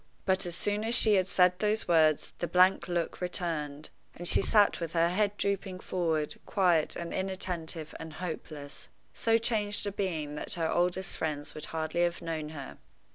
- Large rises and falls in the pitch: No, average, 3.1 semitones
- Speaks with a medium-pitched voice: Yes, medium, 175 Hz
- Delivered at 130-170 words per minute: No, average, 180 wpm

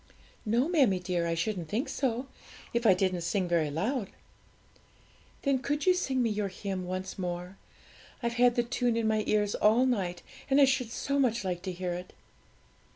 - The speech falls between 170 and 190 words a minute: Yes, average, 185 wpm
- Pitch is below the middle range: No, high, 210 Hz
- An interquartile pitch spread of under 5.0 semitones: No, wide, 5.4 semitones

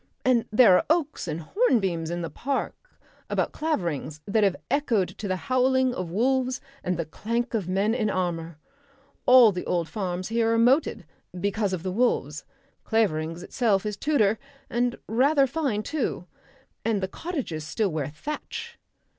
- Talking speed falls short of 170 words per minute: Yes, average, 160 wpm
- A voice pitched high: Yes, high, 215 Hz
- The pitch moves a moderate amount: No, wide, 6.1 semitones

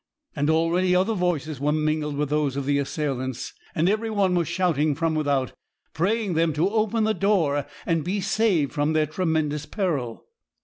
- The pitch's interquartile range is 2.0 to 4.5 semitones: Yes, average, 4.1 semitones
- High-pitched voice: No, medium, 160 Hz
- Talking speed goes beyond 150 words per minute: Yes, average, 175 wpm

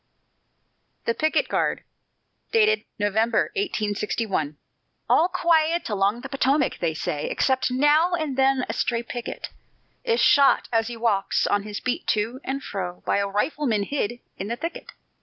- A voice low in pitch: No, high, 240 Hz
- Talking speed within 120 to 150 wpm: Yes, average, 145 wpm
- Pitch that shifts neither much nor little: No, wide, 5.9 semitones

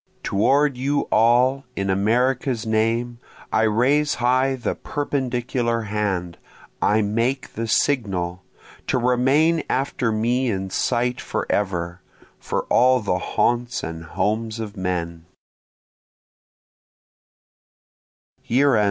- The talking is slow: Yes, slow, 100 wpm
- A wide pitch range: No, average, 4.0 semitones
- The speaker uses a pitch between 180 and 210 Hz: No, low, 115 Hz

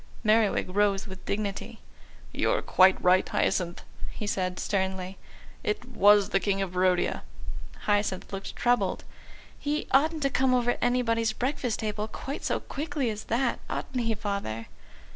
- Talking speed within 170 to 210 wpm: No, average, 145 wpm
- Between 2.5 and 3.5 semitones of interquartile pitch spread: No, average, 4.2 semitones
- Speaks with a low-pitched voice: No, high, 210 Hz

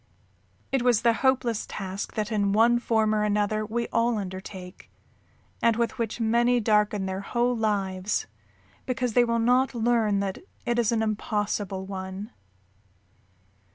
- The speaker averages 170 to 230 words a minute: No, average, 150 wpm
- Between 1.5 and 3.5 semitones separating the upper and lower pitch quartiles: Yes, average, 2.8 semitones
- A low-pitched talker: No, high, 215 Hz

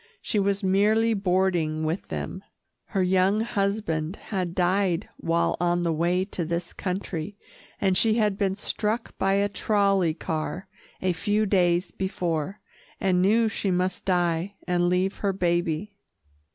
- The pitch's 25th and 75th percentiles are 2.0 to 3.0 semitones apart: Yes, narrow, 2.5 semitones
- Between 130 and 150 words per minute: Yes, average, 145 wpm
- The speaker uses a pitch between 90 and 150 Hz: No, medium, 185 Hz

